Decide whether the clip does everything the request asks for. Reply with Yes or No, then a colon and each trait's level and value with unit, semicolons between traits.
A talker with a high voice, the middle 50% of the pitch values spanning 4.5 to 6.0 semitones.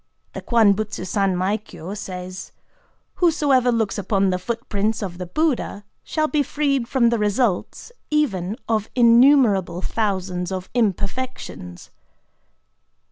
Yes: high, 215 Hz; average, 5.1 semitones